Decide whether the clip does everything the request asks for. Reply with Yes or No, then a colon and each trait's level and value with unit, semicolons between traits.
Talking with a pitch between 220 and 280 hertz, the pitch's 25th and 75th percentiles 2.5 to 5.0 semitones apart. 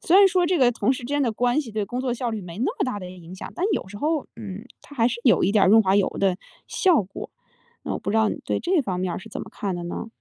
No: high, 225 Hz; wide, 5.4 semitones